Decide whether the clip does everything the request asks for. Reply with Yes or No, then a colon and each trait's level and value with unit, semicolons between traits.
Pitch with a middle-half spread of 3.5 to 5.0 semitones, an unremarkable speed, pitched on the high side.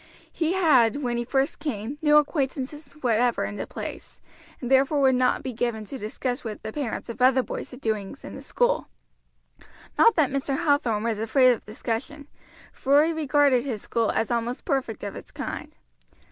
Yes: average, 3.9 semitones; average, 185 wpm; very high, 260 Hz